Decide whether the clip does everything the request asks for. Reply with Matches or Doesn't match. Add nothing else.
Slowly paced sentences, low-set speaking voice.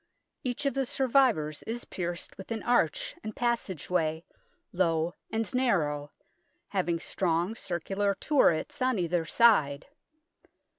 Doesn't match